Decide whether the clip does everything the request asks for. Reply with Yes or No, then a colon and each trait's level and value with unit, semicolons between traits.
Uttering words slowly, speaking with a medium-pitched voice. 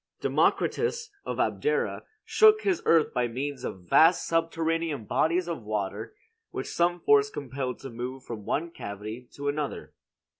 No: average, 145 wpm; medium, 145 Hz